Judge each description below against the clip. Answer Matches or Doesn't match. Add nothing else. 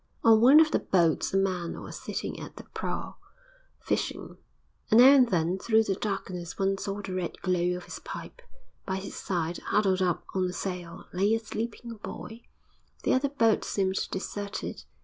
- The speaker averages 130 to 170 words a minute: Doesn't match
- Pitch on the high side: Matches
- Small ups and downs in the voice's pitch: Doesn't match